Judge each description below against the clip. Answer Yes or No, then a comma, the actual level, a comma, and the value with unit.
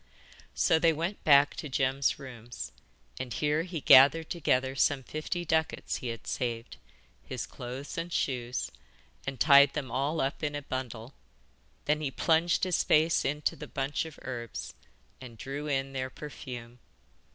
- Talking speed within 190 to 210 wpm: No, average, 155 wpm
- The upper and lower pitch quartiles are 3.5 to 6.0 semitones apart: No, average, 3.0 semitones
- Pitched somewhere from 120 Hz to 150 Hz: Yes, medium, 140 Hz